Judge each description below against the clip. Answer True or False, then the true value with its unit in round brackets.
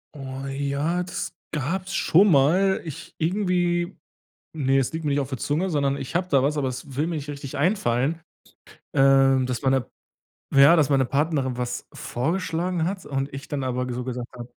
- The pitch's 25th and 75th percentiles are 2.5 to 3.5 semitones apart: False (4.0 semitones)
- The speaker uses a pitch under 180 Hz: True (140 Hz)